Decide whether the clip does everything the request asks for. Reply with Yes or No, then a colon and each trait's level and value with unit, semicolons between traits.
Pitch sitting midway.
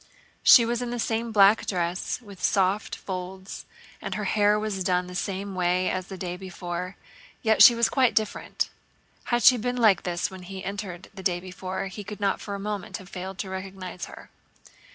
No: high, 195 Hz